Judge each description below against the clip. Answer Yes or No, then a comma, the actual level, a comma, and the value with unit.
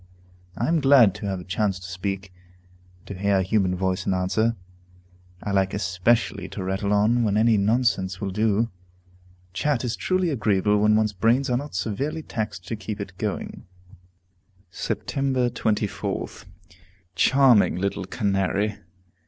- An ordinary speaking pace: Yes, average, 150 wpm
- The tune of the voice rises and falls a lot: No, average, 3.5 semitones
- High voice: No, low, 105 Hz